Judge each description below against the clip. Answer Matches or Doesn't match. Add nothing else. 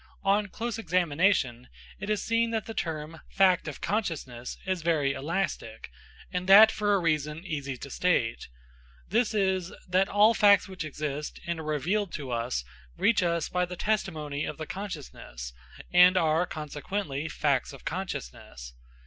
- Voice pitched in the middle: Matches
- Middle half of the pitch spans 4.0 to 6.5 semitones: Matches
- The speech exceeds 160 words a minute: Doesn't match